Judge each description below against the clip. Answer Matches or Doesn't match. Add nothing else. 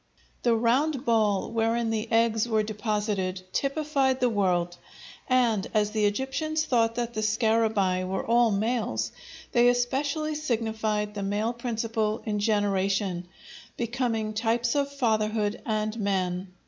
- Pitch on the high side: Matches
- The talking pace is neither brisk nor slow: Doesn't match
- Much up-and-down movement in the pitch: Doesn't match